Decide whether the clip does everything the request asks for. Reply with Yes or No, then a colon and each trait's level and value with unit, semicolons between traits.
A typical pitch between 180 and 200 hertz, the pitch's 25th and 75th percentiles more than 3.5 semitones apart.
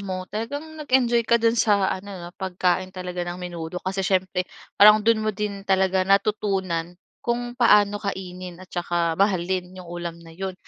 No: high, 190 Hz; average, 2.7 semitones